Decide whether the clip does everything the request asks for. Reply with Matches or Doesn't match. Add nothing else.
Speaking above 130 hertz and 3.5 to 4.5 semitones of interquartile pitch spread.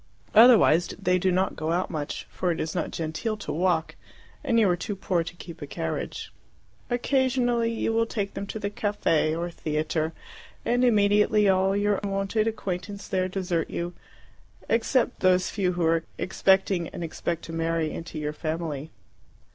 Matches